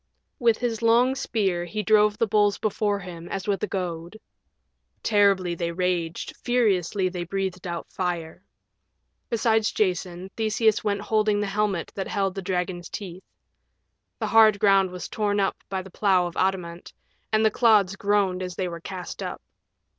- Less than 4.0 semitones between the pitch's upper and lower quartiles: Yes, average, 2.8 semitones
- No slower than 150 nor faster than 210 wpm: Yes, average, 160 wpm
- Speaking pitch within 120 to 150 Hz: No, high, 195 Hz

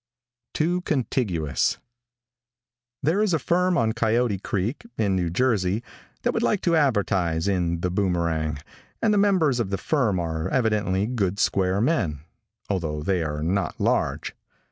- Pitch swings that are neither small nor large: No, wide, 6.7 semitones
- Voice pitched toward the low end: Yes, low, 100 Hz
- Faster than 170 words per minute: No, average, 145 wpm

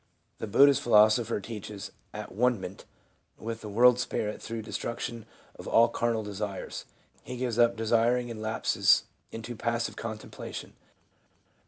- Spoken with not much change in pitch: Yes, narrow, 1.7 semitones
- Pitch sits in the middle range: No, low, 115 Hz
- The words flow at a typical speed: Yes, average, 145 wpm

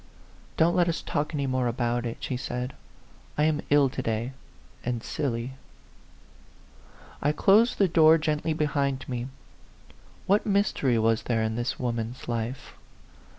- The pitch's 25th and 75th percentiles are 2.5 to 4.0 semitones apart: No, average, 4.5 semitones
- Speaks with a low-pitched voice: Yes, low, 130 Hz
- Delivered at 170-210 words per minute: No, average, 150 wpm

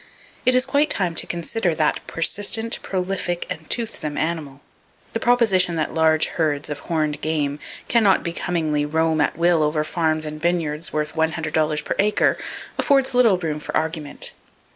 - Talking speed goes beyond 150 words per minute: Yes, average, 165 wpm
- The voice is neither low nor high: Yes, medium, 160 Hz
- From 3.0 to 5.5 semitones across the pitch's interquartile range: Yes, average, 3.5 semitones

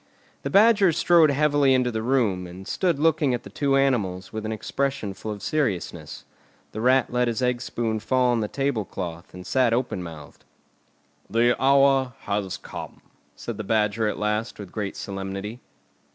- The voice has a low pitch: Yes, low, 115 Hz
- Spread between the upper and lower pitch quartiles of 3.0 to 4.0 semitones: No, average, 5.0 semitones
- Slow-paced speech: No, average, 175 wpm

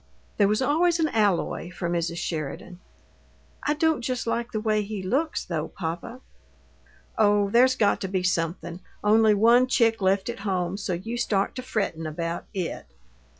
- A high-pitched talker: Yes, high, 205 Hz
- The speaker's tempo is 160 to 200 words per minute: Yes, average, 165 wpm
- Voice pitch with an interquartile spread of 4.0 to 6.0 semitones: Yes, average, 4.9 semitones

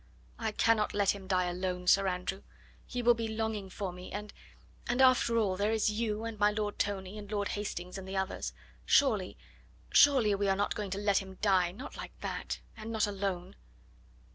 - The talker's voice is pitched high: Yes, high, 205 Hz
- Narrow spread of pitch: Yes, narrow, 2.2 semitones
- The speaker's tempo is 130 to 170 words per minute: No, average, 195 wpm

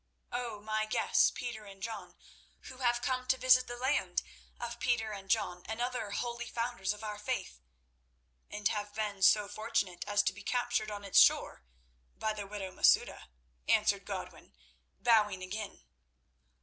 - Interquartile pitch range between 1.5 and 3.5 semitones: Yes, average, 2.8 semitones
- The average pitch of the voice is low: No, high, 215 Hz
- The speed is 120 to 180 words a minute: Yes, average, 160 wpm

